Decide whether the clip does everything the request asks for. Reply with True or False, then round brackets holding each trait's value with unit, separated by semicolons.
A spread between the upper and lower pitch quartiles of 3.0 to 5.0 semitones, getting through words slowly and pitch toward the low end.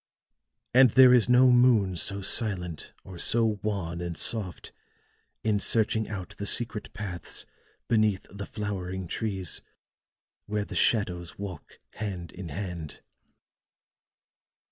True (3.5 semitones; 120 wpm; 100 Hz)